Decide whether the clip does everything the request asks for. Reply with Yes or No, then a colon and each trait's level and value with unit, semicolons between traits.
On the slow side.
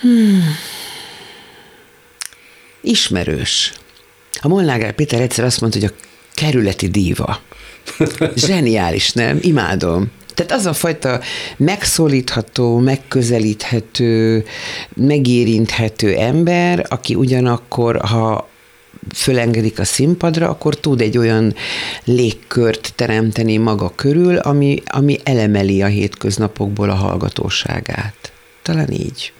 Yes: slow, 95 wpm